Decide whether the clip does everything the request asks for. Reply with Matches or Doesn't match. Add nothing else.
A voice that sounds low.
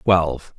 Matches